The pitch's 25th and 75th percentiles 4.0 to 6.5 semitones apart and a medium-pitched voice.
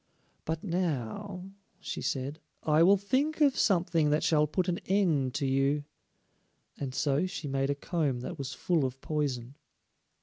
Yes: average, 4.9 semitones; medium, 150 Hz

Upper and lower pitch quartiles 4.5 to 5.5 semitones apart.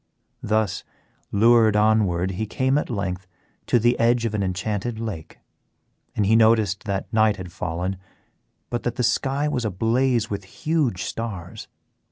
No: average, 3.6 semitones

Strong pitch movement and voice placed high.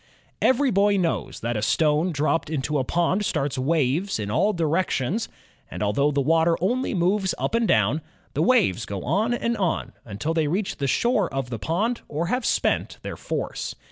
No: wide, 6.7 semitones; medium, 165 Hz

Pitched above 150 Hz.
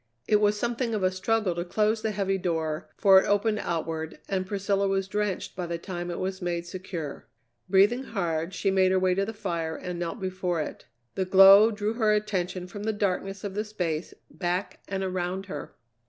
Yes: high, 190 Hz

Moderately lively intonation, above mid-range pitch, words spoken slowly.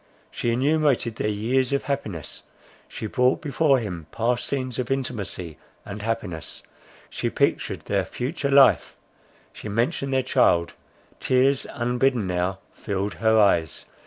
No: average, 4.7 semitones; low, 120 Hz; slow, 130 wpm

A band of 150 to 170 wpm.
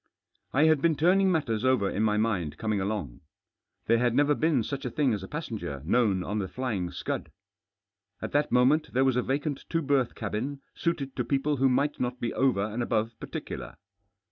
No: average, 195 wpm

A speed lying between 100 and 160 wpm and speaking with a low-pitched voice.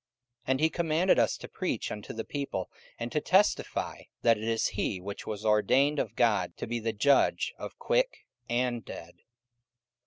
No: average, 180 wpm; low, 120 Hz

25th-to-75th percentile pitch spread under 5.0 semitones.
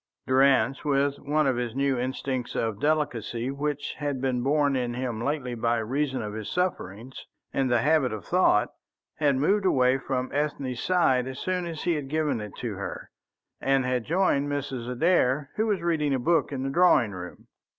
Yes: average, 3.3 semitones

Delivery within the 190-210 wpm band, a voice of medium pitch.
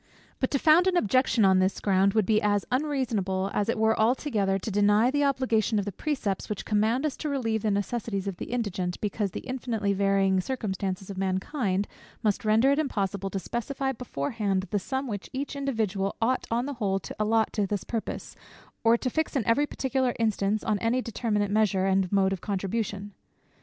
No: average, 195 wpm; high, 215 Hz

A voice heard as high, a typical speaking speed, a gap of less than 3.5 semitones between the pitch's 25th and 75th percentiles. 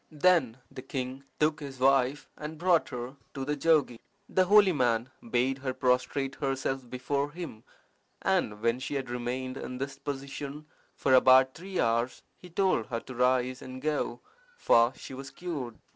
No: low, 135 Hz; average, 165 wpm; average, 2.7 semitones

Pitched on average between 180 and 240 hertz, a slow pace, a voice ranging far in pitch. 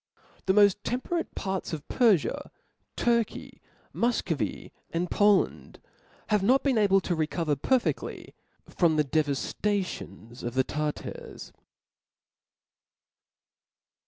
Yes: high, 190 Hz; slow, 100 wpm; wide, 5.9 semitones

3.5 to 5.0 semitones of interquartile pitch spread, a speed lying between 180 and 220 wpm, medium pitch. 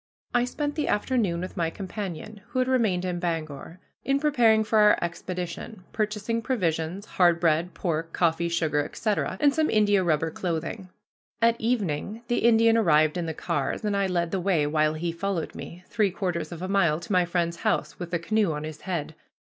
Yes: average, 4.5 semitones; average, 190 wpm; medium, 180 Hz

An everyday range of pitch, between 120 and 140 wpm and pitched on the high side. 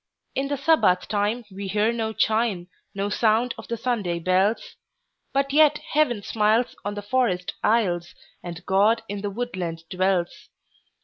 Yes: average, 4.2 semitones; slow, 135 wpm; high, 210 Hz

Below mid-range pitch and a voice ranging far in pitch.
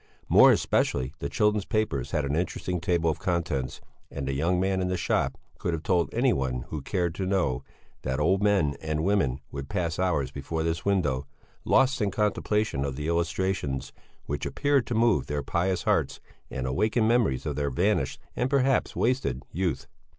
Yes: very low, 85 Hz; wide, 6.1 semitones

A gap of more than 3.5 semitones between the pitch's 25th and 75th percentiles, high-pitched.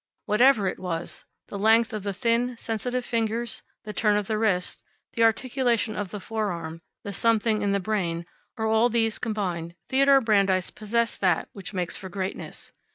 No: average, 3.1 semitones; high, 215 Hz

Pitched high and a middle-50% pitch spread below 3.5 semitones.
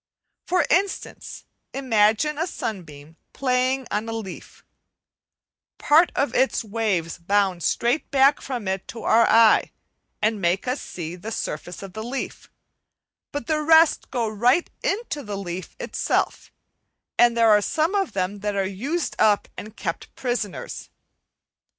No: high, 225 Hz; wide, 5.6 semitones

